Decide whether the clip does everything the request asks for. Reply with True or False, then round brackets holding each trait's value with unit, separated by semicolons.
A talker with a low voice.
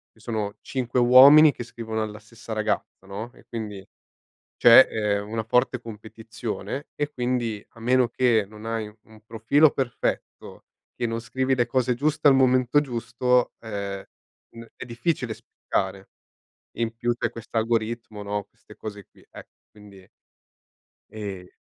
True (115 Hz)